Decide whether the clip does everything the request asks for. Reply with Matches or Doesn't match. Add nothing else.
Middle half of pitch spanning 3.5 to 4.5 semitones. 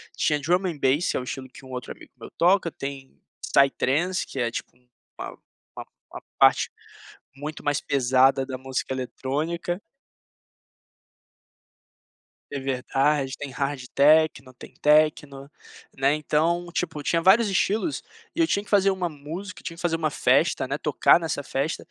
Matches